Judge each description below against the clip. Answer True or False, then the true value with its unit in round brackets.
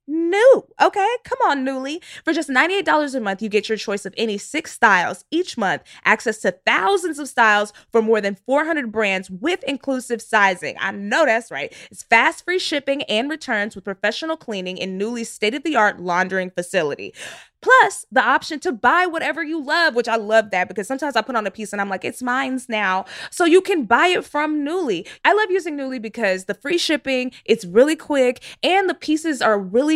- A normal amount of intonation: False (7.3 semitones)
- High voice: True (260 Hz)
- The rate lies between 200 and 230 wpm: True (205 wpm)